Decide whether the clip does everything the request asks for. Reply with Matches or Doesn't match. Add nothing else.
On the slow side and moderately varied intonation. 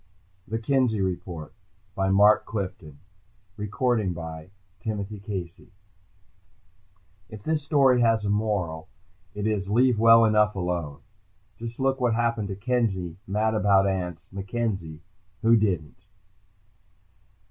Matches